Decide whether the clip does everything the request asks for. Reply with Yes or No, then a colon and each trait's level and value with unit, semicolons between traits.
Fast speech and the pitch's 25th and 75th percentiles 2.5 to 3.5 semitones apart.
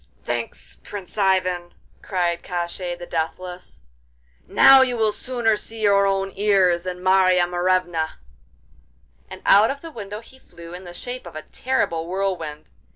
No: average, 150 wpm; average, 3.1 semitones